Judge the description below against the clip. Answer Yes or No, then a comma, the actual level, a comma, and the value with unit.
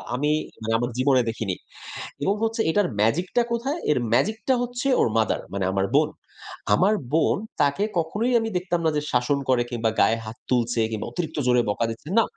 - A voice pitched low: No, medium, 145 Hz